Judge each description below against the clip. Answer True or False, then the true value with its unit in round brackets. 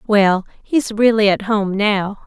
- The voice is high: True (205 Hz)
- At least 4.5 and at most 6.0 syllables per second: False (3.6 syllables/s)